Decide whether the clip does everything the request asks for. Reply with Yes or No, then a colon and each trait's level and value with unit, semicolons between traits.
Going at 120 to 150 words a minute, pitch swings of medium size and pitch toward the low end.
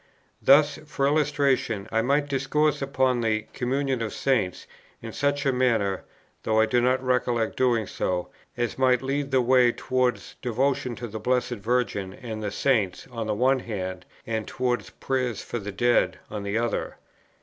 No: average, 170 wpm; average, 3.3 semitones; low, 125 Hz